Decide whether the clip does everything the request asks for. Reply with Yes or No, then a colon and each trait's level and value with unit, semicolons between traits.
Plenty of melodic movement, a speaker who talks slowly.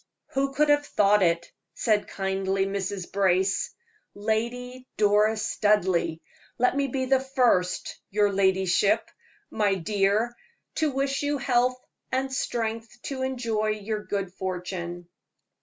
No: average, 4.7 semitones; slow, 125 wpm